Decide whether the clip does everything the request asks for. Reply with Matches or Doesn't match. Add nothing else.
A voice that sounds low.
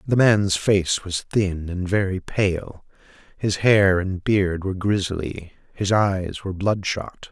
Matches